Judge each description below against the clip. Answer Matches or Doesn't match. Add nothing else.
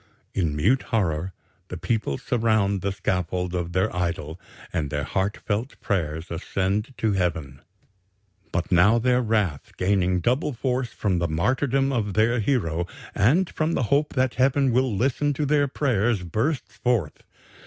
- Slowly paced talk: Doesn't match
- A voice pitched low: Matches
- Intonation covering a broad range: Matches